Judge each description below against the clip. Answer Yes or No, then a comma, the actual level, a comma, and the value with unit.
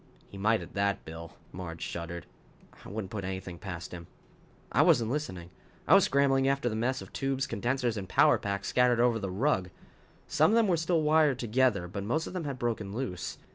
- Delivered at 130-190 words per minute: No, fast, 205 wpm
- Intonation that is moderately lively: No, wide, 6.2 semitones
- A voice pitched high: No, low, 115 Hz